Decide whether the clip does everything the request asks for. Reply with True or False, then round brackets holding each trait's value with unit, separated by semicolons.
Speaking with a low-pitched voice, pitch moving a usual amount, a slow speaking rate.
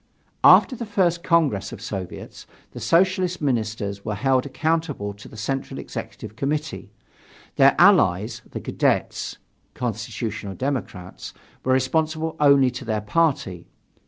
False (130 Hz; 6.9 semitones; 125 wpm)